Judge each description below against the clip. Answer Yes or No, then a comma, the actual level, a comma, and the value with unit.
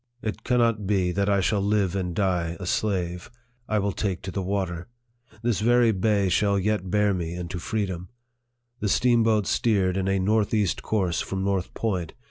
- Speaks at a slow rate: No, average, 180 wpm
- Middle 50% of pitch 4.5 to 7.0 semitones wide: No, narrow, 2.6 semitones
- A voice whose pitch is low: Yes, low, 100 Hz